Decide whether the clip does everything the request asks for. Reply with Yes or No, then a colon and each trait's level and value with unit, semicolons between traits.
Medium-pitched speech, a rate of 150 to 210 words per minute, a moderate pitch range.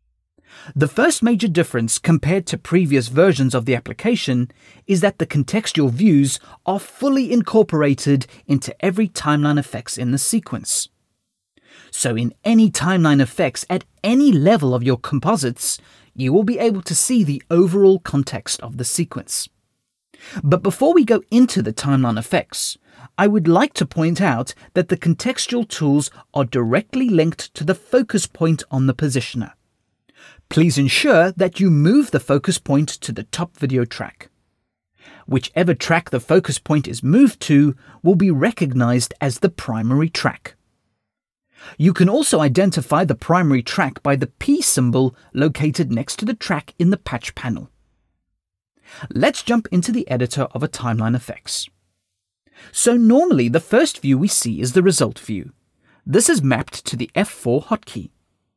No: medium, 155 Hz; average, 155 wpm; wide, 6.8 semitones